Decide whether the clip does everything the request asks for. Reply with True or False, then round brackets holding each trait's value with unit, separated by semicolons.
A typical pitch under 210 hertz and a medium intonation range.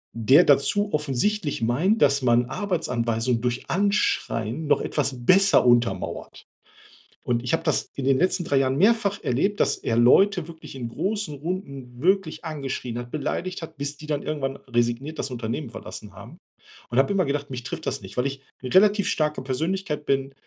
False (140 Hz; 6.3 semitones)